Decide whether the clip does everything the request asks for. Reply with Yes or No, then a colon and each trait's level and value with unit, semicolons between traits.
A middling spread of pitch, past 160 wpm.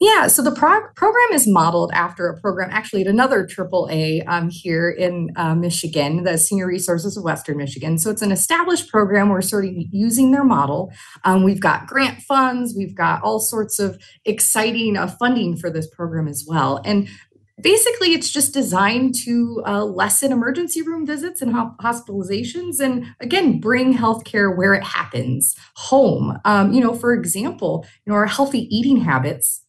No: wide, 6.3 semitones; average, 175 wpm